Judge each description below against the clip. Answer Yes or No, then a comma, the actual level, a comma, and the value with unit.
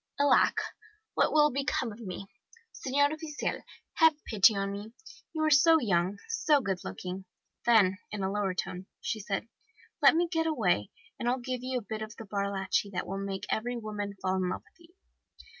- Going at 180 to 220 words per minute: Yes, average, 190 wpm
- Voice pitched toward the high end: Yes, high, 215 Hz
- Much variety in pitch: Yes, wide, 6.5 semitones